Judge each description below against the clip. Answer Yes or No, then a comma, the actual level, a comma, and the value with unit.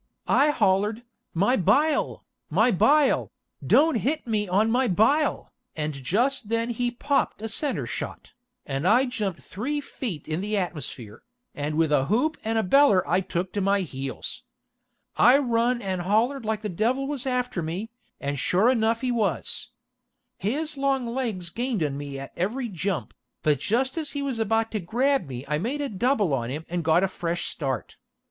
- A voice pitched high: Yes, high, 215 Hz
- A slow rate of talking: No, average, 180 wpm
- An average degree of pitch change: No, wide, 6.5 semitones